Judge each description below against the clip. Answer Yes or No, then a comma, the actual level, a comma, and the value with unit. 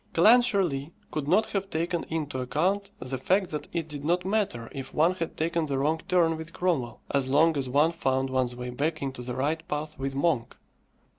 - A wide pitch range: No, average, 4.1 semitones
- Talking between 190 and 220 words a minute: Yes, average, 200 wpm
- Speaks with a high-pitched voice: No, medium, 155 Hz